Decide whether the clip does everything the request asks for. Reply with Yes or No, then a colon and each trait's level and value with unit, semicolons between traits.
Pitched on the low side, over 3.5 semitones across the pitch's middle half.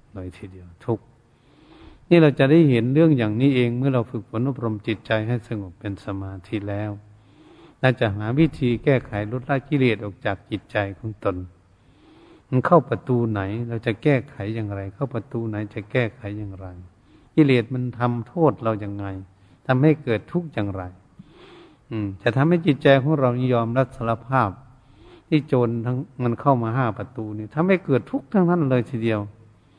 Yes: low, 115 Hz; average, 4.3 semitones